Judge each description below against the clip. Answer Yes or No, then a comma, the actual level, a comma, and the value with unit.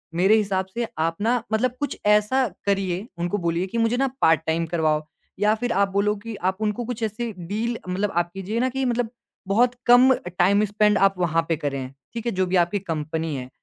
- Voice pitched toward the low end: No, high, 200 Hz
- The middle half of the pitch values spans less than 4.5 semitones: No, average, 5.0 semitones